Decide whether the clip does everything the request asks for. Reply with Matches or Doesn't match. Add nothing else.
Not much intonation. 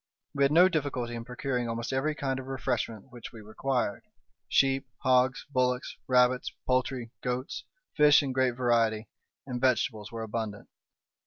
Matches